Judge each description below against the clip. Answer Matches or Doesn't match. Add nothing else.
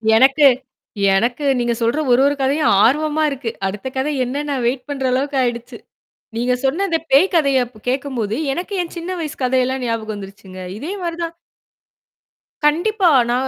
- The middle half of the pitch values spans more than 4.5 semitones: Doesn't match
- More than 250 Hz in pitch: Matches